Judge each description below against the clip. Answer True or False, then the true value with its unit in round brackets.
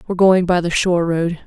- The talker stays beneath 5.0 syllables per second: False (6.4 syllables/s)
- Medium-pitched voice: True (175 Hz)